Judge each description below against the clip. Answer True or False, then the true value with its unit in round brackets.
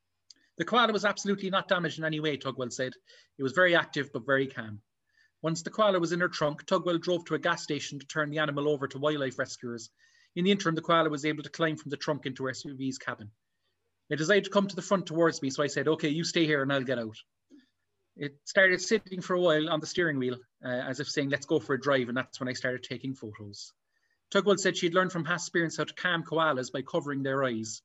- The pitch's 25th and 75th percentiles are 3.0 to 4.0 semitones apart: False (4.8 semitones)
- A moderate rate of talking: False (250 wpm)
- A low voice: False (155 Hz)